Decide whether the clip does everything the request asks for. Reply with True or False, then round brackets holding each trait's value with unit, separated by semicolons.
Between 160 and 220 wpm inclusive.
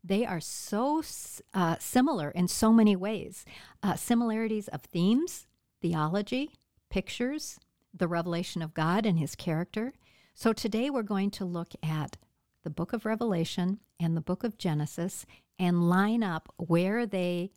False (145 wpm)